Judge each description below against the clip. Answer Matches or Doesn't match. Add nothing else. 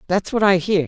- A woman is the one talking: Matches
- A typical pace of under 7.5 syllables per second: Matches